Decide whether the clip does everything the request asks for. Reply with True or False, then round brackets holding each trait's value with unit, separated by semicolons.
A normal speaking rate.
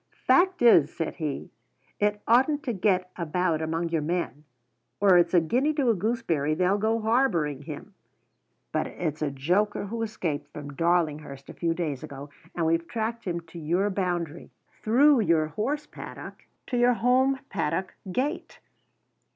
True (160 wpm)